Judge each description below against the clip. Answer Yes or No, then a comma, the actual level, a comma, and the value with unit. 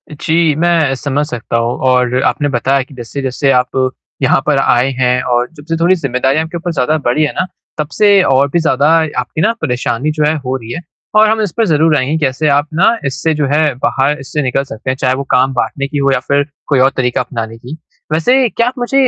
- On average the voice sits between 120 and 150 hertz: Yes, medium, 140 Hz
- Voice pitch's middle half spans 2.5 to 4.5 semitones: Yes, average, 3.6 semitones